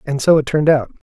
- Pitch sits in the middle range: Yes, medium, 145 Hz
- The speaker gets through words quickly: Yes, fast, 270 wpm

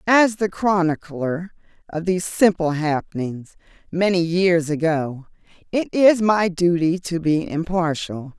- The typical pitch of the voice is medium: Yes, medium, 175 Hz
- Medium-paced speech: No, slow, 120 wpm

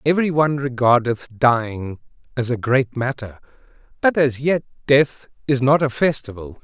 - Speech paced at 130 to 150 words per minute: Yes, average, 145 wpm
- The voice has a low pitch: Yes, low, 130 Hz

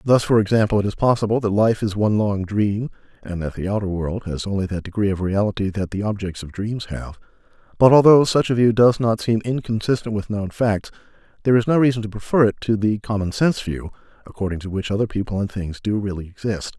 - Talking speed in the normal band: No, fast, 225 wpm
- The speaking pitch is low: Yes, low, 105 Hz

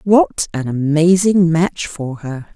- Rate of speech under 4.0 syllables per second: Yes, 3.4 syllables/s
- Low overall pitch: No, medium, 165 Hz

